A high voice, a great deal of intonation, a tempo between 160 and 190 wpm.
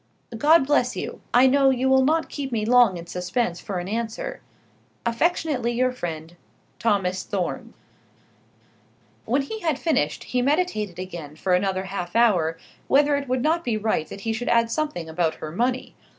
Yes: high, 230 Hz; wide, 6.6 semitones; average, 170 wpm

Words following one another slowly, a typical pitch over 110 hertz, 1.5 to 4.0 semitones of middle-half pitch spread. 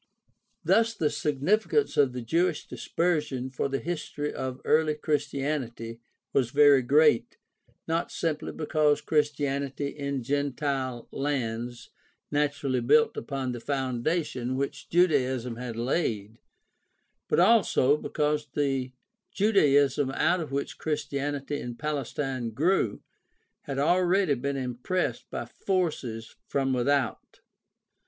Yes: slow, 115 wpm; medium, 140 Hz; average, 3.0 semitones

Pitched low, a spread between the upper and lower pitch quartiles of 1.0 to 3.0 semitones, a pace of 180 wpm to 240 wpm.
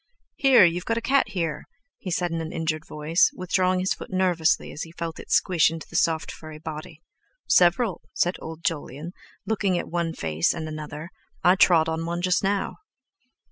No: medium, 170 Hz; narrow, 2.5 semitones; average, 185 wpm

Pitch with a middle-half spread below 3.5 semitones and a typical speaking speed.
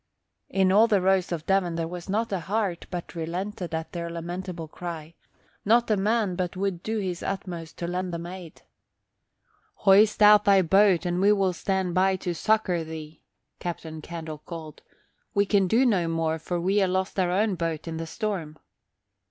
Yes: average, 2.8 semitones; average, 185 wpm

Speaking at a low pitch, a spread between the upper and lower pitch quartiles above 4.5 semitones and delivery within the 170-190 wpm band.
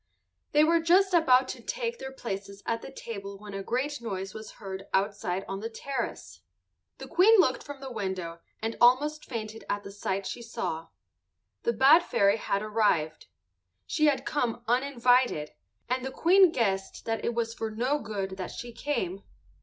No: high, 230 Hz; wide, 5.6 semitones; average, 175 wpm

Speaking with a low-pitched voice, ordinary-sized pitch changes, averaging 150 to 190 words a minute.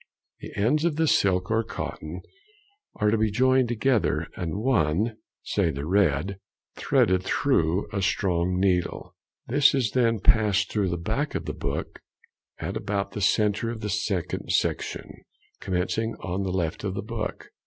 Yes: low, 100 Hz; average, 3.8 semitones; average, 160 wpm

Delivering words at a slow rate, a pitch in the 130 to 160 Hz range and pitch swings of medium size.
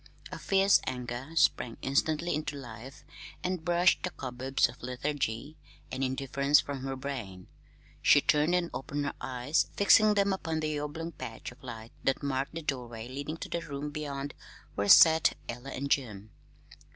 No: average, 165 wpm; medium, 140 Hz; average, 3.7 semitones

